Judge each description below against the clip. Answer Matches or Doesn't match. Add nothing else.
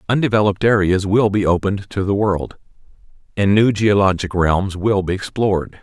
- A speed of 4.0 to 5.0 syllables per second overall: Doesn't match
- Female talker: Doesn't match